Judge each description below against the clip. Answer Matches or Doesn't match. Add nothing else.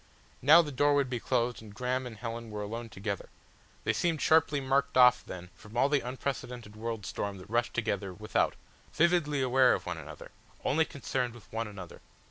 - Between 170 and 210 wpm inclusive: Matches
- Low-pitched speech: Matches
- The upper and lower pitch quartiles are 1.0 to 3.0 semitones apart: Doesn't match